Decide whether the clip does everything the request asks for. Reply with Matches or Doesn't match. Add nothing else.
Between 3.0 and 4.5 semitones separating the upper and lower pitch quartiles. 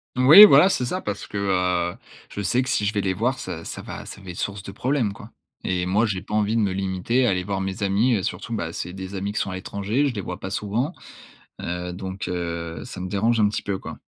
Matches